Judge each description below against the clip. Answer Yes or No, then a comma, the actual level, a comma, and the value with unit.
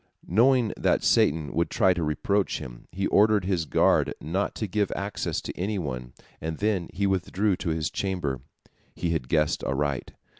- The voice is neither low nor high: No, very low, 90 Hz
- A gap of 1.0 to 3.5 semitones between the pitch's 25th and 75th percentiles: No, average, 4.8 semitones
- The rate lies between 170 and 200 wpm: Yes, average, 175 wpm